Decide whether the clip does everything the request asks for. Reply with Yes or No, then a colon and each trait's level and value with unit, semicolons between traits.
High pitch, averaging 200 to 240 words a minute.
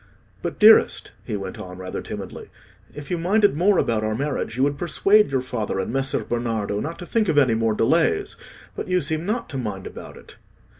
No: low, 135 Hz; fast, 205 wpm